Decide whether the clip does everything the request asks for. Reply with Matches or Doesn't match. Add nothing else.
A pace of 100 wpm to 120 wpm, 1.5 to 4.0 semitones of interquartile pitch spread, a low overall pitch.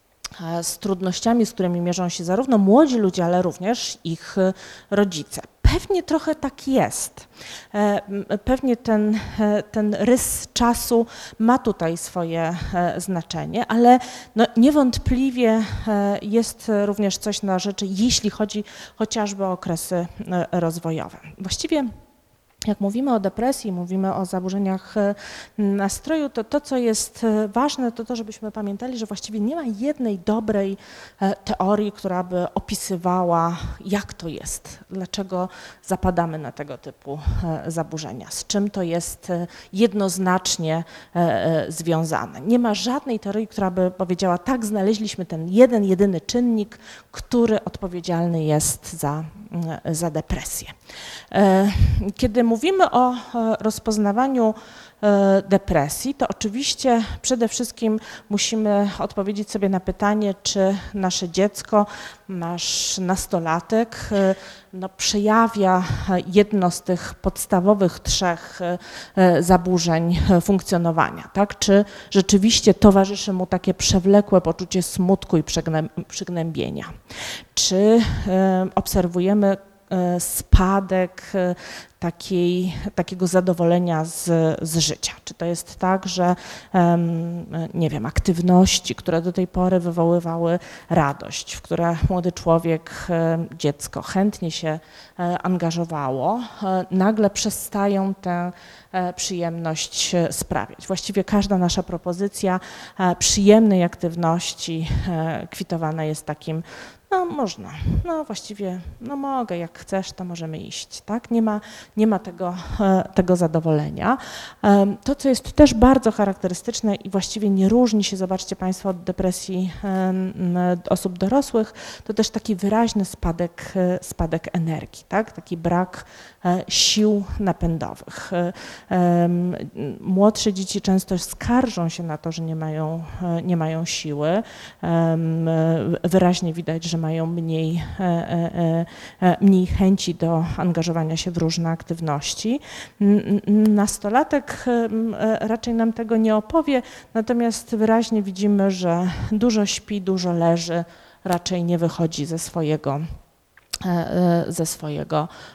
Doesn't match